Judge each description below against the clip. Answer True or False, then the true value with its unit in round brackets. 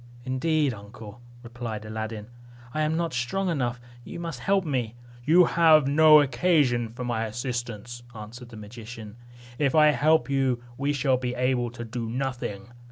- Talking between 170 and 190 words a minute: False (160 wpm)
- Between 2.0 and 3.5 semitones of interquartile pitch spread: False (4.3 semitones)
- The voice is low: True (125 Hz)